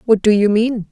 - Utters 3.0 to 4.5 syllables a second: No, 5.1 syllables/s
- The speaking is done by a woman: Yes, female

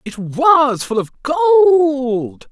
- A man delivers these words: Yes, male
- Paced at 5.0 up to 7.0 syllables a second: No, 3.8 syllables/s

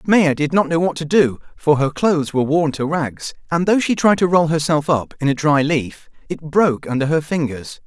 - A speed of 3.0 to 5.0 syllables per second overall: No, 5.2 syllables/s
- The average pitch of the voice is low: No, medium, 155 Hz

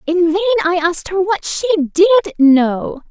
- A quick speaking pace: No, average, 175 wpm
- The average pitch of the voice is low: No, very high, 355 Hz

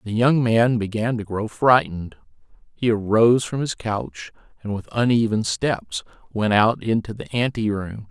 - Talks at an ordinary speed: Yes, average, 155 wpm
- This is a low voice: Yes, low, 110 Hz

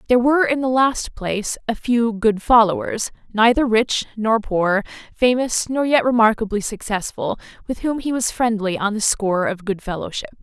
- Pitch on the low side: No, high, 225 Hz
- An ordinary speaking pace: Yes, average, 175 wpm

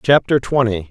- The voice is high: No, low, 120 Hz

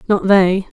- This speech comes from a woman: Yes, female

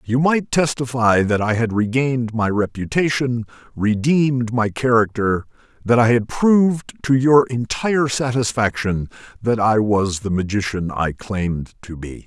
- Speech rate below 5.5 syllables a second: Yes, 4.5 syllables/s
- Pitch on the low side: Yes, low, 115 Hz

